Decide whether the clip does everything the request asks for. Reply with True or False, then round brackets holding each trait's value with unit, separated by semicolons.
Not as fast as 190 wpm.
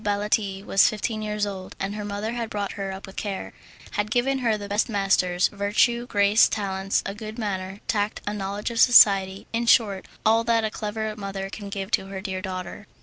False (205 wpm)